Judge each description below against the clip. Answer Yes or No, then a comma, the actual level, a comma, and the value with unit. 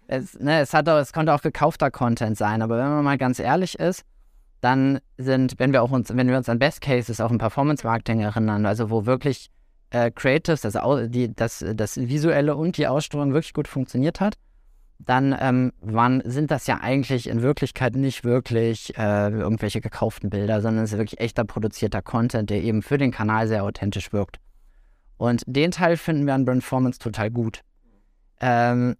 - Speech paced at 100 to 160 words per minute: No, fast, 190 wpm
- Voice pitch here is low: Yes, low, 120 Hz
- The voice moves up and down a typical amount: Yes, average, 3.7 semitones